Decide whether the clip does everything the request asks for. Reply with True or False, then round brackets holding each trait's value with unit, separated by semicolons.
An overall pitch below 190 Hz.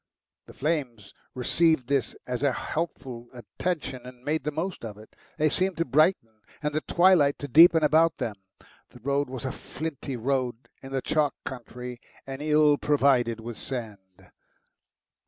True (135 Hz)